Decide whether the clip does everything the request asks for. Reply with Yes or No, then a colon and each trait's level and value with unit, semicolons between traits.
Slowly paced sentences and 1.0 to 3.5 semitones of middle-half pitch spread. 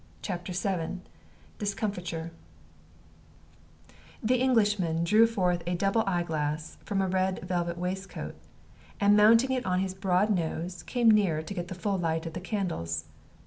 No: average, 145 wpm; average, 3.1 semitones